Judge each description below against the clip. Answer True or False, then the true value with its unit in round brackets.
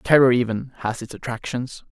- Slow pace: False (155 wpm)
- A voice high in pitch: False (125 Hz)